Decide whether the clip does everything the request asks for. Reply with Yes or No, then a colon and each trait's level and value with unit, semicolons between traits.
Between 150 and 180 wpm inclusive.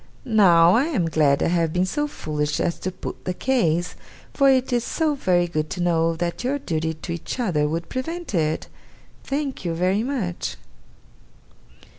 Yes: average, 175 wpm